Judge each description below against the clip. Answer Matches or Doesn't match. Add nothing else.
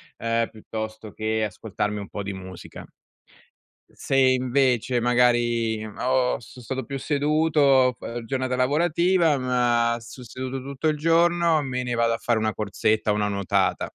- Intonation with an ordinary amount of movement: Matches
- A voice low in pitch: Matches